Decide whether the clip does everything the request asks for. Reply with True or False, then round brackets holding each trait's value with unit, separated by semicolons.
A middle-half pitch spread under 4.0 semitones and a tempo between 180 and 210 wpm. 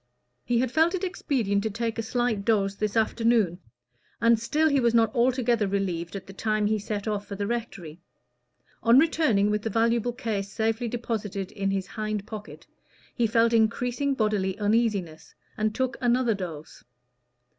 False (2.9 semitones; 165 wpm)